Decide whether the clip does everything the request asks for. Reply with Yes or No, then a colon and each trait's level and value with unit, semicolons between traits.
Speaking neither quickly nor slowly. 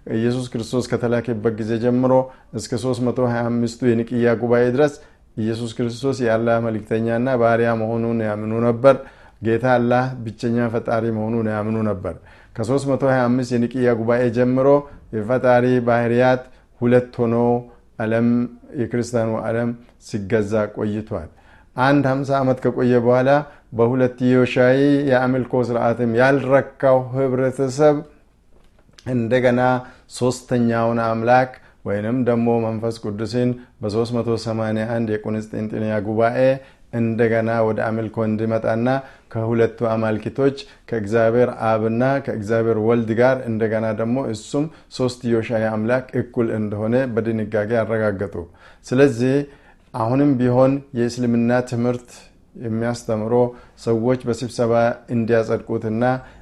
Yes: average, 95 wpm